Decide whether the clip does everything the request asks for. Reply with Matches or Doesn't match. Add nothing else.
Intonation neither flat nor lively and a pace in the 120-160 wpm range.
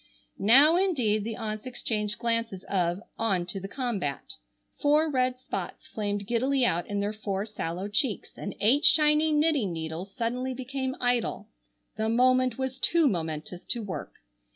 Matches